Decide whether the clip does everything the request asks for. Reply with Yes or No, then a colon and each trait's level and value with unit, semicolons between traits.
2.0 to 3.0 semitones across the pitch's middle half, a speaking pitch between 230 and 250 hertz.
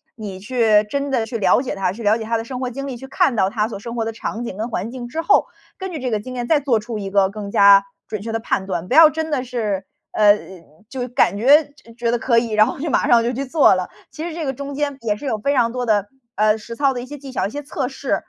No: average, 4.0 semitones; high, 235 Hz